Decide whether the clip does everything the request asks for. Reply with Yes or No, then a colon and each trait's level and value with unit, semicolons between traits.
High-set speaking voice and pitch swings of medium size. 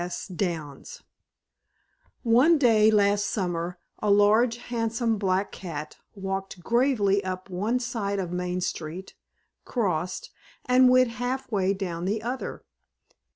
Yes: high, 200 Hz; average, 4.3 semitones